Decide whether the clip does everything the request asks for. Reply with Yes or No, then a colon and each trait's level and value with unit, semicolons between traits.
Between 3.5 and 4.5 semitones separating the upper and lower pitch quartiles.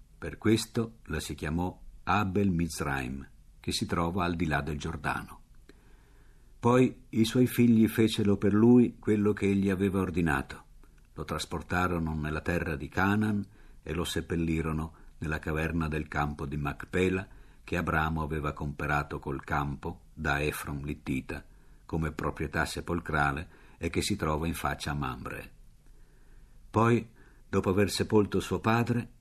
No: average, 5.2 semitones